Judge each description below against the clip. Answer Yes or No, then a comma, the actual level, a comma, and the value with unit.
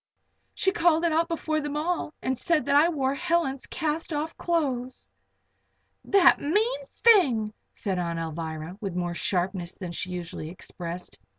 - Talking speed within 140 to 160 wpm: Yes, average, 155 wpm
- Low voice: No, very high, 275 Hz